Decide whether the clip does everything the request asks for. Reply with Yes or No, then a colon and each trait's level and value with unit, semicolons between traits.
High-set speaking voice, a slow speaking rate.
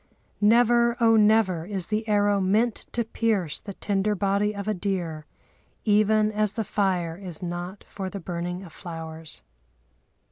No: high, 200 Hz; average, 150 wpm